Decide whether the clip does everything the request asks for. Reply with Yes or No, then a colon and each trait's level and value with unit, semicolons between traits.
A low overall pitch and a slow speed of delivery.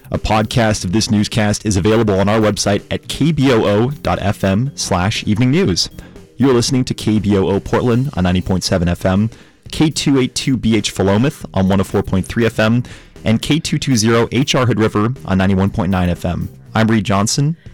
Yes: low, 110 Hz; slow, 130 wpm